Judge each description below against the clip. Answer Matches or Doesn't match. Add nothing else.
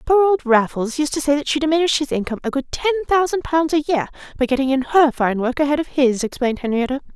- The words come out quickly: Matches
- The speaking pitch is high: Matches